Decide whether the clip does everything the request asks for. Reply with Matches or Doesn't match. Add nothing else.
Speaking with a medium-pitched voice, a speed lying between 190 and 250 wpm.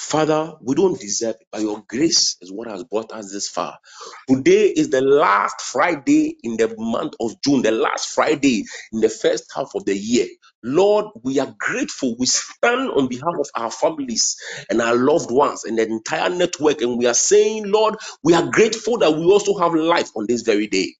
Matches